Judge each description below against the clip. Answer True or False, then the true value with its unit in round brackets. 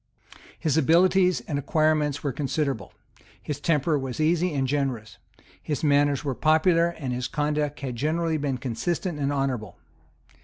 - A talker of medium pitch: True (145 Hz)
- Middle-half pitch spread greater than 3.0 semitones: False (2.7 semitones)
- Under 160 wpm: True (145 wpm)